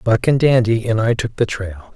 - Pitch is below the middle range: Yes, low, 110 Hz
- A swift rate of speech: Yes, fast, 245 wpm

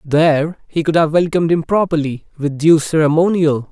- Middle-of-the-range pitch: Yes, medium, 155 Hz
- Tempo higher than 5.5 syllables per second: No, 5.3 syllables/s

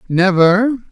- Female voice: No, male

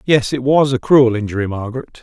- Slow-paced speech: No, fast, 205 wpm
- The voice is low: Yes, low, 125 Hz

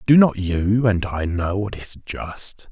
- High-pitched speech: No, low, 100 Hz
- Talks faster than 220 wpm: No, average, 200 wpm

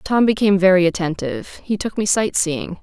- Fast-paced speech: No, average, 170 wpm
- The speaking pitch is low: No, high, 190 Hz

